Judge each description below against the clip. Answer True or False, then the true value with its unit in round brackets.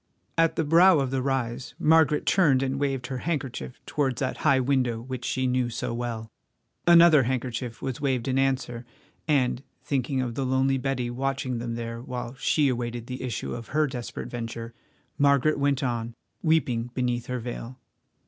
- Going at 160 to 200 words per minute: True (170 wpm)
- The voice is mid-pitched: False (130 Hz)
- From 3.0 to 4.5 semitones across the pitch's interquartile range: False (2.4 semitones)